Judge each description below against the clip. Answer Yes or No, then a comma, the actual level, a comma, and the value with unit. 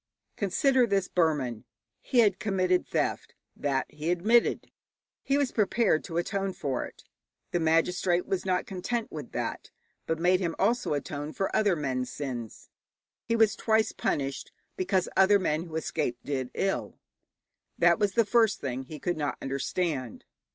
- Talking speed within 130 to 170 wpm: Yes, average, 155 wpm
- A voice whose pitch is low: No, medium, 180 Hz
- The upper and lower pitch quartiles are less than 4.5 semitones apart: No, wide, 5.4 semitones